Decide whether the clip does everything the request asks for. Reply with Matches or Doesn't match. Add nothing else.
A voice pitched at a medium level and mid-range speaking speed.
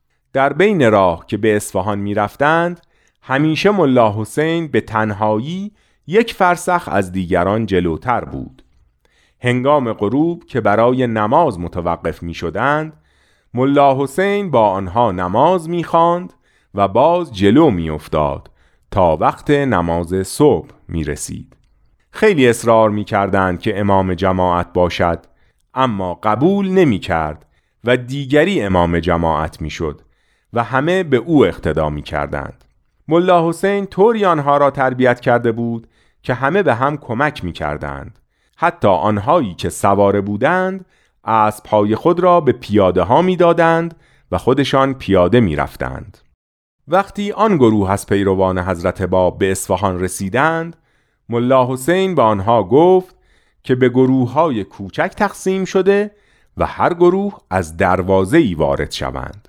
Doesn't match